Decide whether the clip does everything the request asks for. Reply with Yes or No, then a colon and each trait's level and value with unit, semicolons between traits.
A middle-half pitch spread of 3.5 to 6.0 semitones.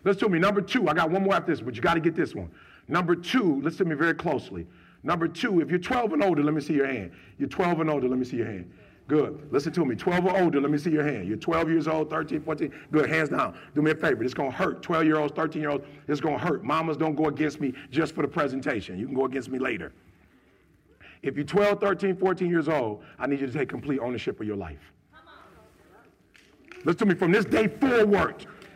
Yes: average, 4.3 semitones